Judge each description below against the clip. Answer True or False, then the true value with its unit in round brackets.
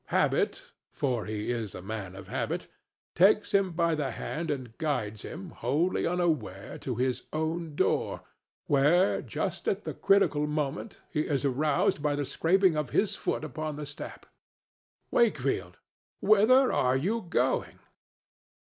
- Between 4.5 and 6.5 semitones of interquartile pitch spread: True (5.3 semitones)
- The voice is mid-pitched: True (150 Hz)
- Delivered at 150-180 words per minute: False (135 wpm)